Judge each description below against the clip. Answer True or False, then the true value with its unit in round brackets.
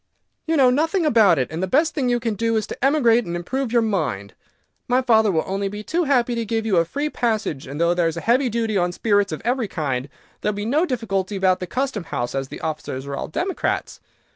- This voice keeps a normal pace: False (245 wpm)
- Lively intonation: True (6.3 semitones)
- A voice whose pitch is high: True (220 Hz)